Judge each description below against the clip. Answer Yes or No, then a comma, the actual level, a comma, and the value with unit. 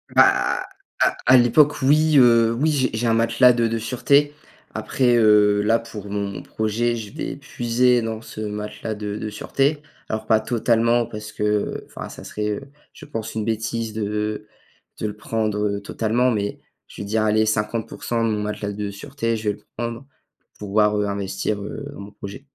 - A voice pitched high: No, low, 110 Hz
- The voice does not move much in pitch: Yes, narrow, 2.3 semitones